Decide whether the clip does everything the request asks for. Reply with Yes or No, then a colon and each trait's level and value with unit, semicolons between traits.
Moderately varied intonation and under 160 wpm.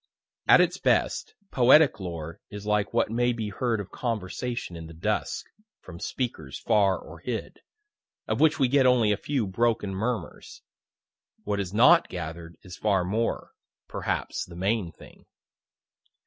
Yes: average, 5.0 semitones; average, 150 wpm